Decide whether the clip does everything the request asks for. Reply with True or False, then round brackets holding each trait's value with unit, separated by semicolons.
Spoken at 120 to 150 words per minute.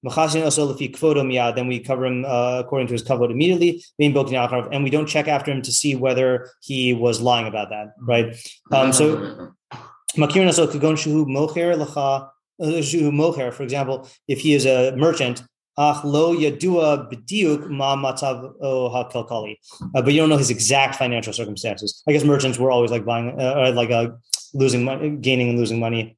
True (135 wpm)